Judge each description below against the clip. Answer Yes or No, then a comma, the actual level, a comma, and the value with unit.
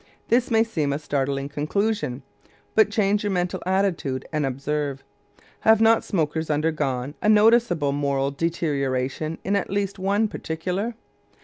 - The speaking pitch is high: No, medium, 160 Hz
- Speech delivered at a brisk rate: No, slow, 135 wpm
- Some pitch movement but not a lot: No, wide, 6.4 semitones